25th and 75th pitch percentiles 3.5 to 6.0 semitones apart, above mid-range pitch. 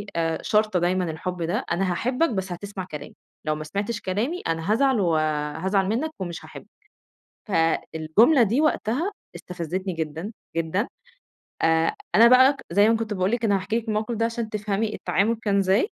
Yes: average, 4.7 semitones; high, 200 Hz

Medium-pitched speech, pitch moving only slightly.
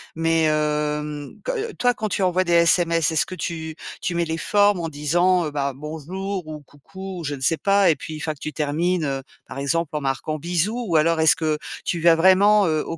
No: medium, 165 Hz; average, 3.2 semitones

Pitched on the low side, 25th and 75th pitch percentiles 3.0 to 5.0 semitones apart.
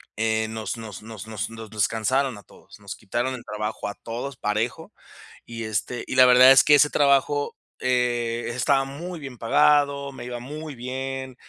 Yes: low, 125 Hz; average, 3.5 semitones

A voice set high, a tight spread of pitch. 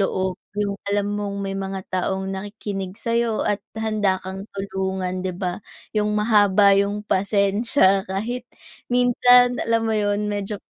Yes: high, 205 Hz; narrow, 2.0 semitones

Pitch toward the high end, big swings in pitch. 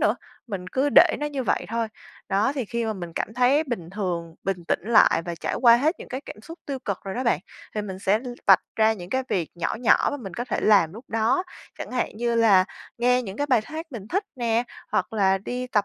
No: high, 225 Hz; average, 4.7 semitones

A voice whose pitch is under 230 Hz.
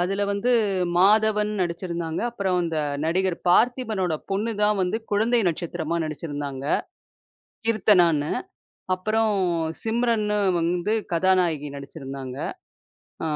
Yes: medium, 185 Hz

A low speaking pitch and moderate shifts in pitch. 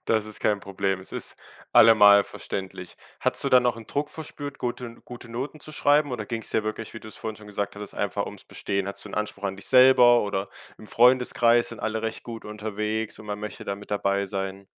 Yes: low, 110 Hz; average, 3.0 semitones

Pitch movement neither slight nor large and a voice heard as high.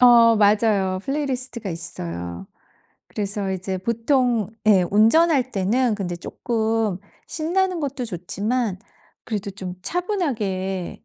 Yes: average, 5.0 semitones; high, 220 Hz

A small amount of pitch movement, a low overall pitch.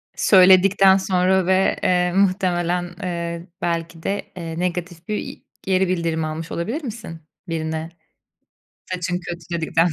No: narrow, 2.0 semitones; medium, 180 Hz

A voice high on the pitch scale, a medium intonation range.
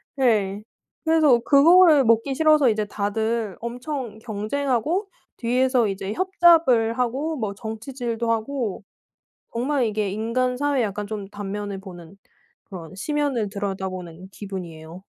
Yes: high, 230 Hz; average, 5.0 semitones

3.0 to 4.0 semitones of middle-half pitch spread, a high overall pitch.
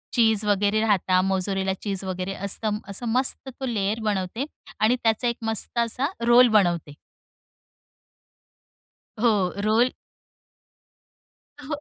Yes: average, 3.3 semitones; high, 215 Hz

